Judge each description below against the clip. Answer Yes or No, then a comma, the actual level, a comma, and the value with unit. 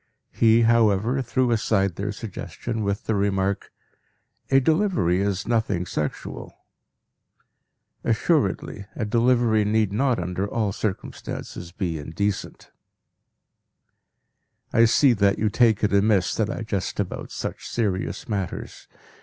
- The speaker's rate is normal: No, slow, 120 wpm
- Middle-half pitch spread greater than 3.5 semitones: No, average, 2.9 semitones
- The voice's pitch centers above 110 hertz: No, low, 105 Hz